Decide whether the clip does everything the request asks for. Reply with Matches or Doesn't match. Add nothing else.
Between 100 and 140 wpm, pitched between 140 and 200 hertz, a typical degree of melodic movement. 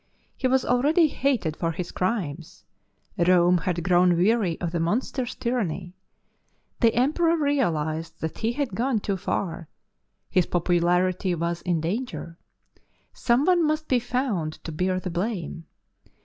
Doesn't match